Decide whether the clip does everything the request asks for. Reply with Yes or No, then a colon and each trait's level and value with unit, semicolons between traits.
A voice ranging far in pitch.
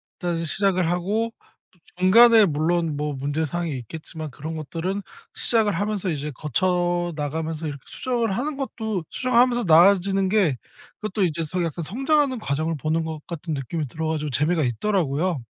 No: average, 4.5 semitones